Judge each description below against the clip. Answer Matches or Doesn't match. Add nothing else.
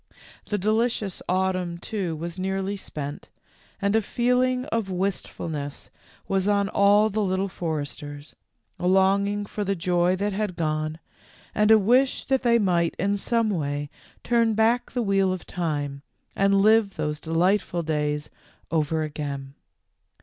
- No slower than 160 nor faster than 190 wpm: Doesn't match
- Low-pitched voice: Doesn't match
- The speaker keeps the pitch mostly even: Doesn't match